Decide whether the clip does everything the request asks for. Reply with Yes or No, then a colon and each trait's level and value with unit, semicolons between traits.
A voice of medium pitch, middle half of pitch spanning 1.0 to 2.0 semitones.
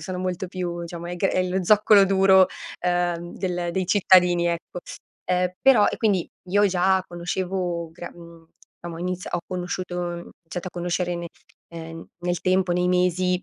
Yes: medium, 180 Hz; narrow, 1.3 semitones